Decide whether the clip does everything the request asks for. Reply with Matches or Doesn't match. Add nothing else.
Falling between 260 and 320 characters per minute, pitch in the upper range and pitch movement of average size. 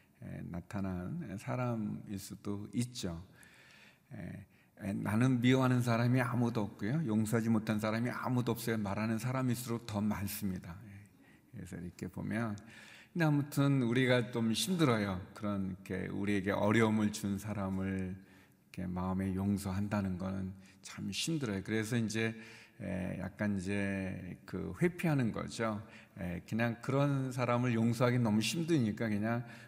Doesn't match